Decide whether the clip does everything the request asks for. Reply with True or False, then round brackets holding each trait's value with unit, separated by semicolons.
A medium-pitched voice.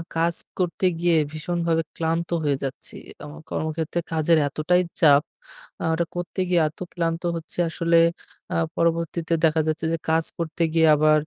True (165 Hz)